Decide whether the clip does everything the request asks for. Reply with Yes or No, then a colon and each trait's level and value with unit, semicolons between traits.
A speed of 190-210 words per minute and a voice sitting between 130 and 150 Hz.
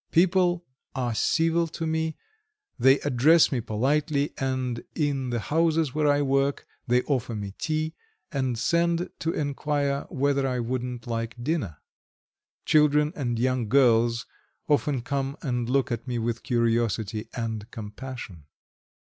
No: slow, 135 wpm; low, 135 Hz